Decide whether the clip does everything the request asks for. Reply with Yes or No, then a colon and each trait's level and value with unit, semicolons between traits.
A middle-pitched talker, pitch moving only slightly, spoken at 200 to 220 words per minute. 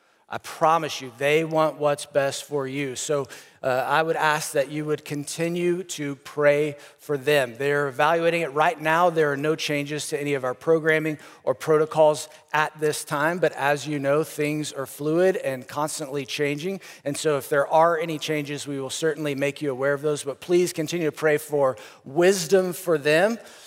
No: medium, 150 Hz; narrow, 1.7 semitones; average, 190 wpm